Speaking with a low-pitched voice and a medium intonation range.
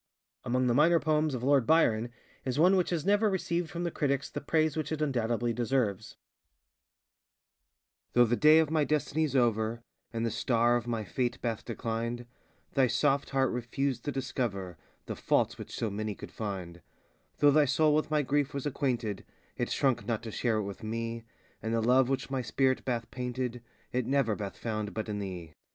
Yes: low, 125 Hz; average, 4.0 semitones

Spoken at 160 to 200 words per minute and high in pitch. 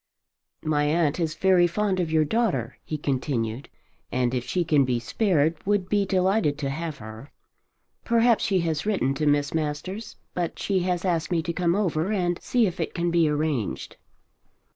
No: average, 180 wpm; medium, 165 Hz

